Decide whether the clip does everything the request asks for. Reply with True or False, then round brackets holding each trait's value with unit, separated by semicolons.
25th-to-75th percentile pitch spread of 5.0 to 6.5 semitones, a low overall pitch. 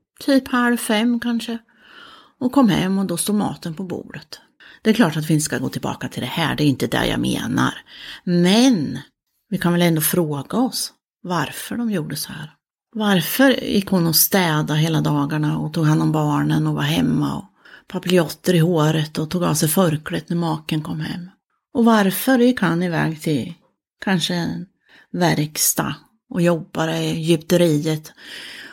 False (5.3 semitones; 175 Hz)